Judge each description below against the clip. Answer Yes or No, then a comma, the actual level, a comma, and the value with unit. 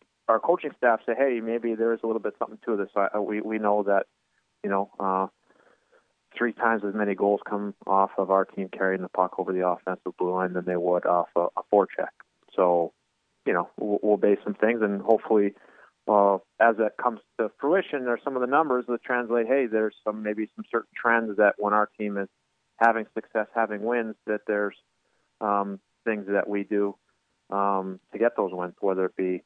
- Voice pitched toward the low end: Yes, low, 105 Hz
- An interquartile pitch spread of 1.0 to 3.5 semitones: Yes, narrow, 2.6 semitones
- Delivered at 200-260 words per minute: Yes, fast, 205 wpm